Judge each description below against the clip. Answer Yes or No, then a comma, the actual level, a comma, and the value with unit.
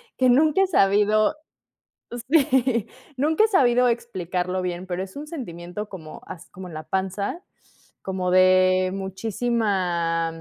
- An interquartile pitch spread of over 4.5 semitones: Yes, average, 5.1 semitones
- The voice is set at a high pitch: Yes, high, 195 Hz